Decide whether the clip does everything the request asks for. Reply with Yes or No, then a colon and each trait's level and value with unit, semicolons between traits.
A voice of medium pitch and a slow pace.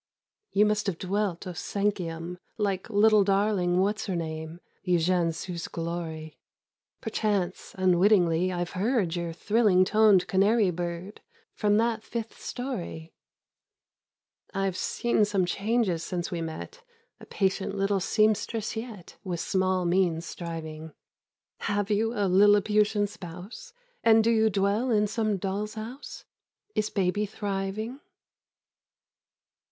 No: high, 195 Hz; slow, 120 wpm